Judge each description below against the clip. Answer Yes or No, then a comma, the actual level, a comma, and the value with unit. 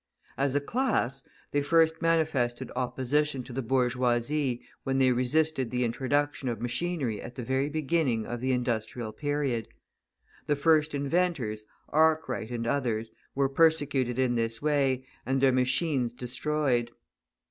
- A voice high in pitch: No, low, 130 Hz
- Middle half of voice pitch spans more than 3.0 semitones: Yes, average, 3.4 semitones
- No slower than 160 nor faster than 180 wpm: No, slow, 135 wpm